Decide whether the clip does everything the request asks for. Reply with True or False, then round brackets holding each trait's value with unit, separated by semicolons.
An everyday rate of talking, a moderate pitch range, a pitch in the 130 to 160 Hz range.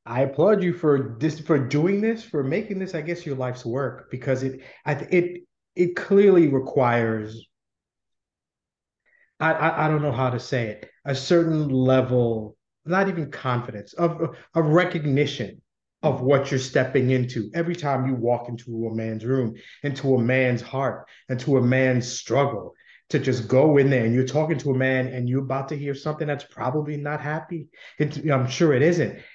True (180 wpm; 3.8 semitones; 140 Hz)